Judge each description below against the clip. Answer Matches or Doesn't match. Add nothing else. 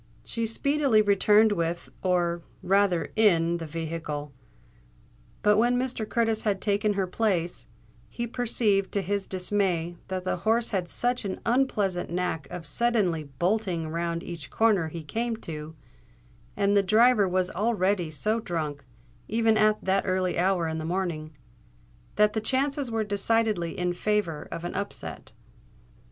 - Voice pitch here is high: Matches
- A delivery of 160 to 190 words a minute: Doesn't match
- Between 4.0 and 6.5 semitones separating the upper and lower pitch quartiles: Matches